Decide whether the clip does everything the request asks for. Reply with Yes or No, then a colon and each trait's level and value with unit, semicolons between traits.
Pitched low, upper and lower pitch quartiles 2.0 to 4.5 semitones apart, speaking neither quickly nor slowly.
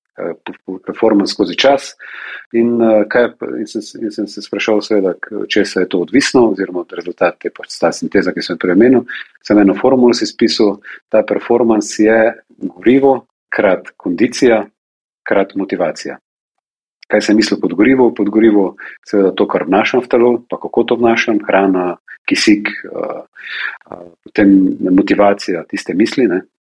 No: low, 105 Hz; average, 3.2 semitones; slow, 130 wpm